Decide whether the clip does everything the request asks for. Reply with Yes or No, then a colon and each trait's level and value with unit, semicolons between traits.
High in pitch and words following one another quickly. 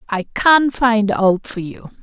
No: high, 225 Hz; average, 180 wpm